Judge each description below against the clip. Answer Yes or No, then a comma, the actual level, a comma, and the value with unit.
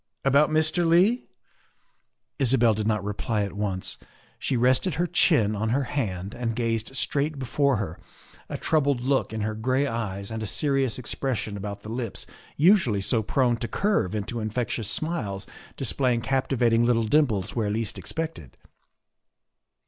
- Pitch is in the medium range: No, low, 120 Hz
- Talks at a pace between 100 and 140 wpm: No, average, 155 wpm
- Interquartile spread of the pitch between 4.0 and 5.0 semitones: Yes, average, 4.6 semitones